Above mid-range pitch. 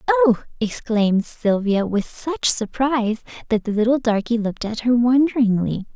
Yes: high, 235 Hz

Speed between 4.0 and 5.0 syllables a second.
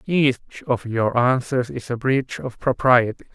Yes: 4.2 syllables/s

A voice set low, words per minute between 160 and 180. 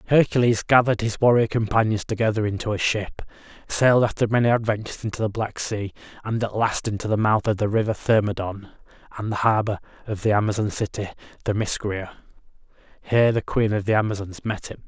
Yes: low, 110 Hz; average, 175 wpm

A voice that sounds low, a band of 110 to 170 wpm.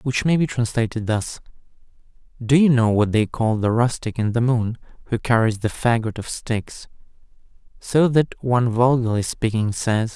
Yes: low, 115 Hz; average, 165 wpm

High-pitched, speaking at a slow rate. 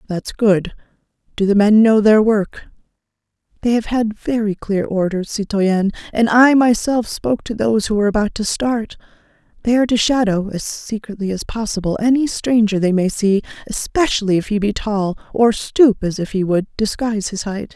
No: high, 215 Hz; average, 170 wpm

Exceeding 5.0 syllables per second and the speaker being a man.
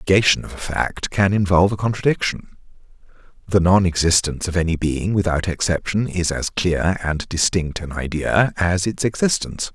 Yes: 5.3 syllables/s; male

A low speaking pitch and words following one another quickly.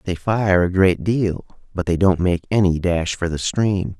Yes: very low, 95 Hz; fast, 210 wpm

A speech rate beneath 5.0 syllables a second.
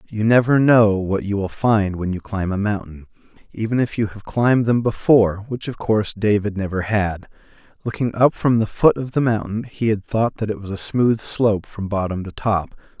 No: 5.1 syllables/s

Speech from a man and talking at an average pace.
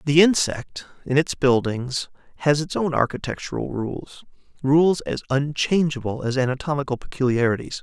No: male; slow, 125 wpm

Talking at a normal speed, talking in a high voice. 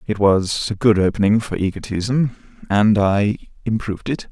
No: average, 155 wpm; low, 105 Hz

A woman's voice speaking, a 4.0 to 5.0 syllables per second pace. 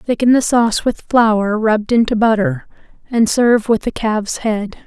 Yes: female; 4.9 syllables/s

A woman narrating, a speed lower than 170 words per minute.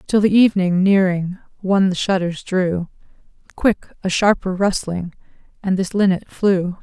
Yes: female; average, 140 wpm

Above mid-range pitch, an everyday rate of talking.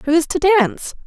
No: very high, 325 Hz; fast, 225 wpm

